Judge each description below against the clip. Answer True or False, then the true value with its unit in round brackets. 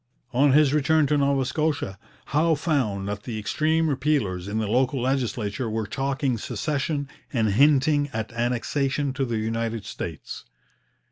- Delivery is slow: False (145 wpm)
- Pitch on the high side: False (130 Hz)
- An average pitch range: True (4.6 semitones)